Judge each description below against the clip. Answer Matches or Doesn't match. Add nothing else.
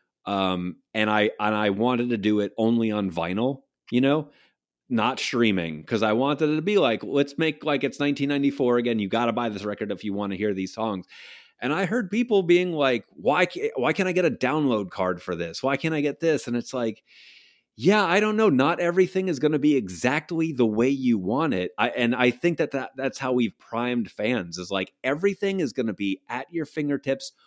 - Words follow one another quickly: Matches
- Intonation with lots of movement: Matches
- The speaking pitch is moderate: Doesn't match